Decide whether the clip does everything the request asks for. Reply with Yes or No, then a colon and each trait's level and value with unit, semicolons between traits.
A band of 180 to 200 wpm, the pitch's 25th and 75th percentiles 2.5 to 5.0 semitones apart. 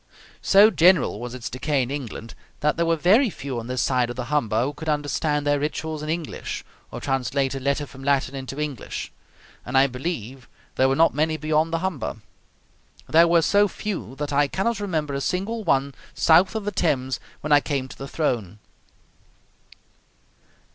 Yes: average, 185 wpm; average, 3.8 semitones